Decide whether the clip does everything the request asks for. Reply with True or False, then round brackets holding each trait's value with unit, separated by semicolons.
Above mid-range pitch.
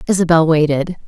False (165 Hz)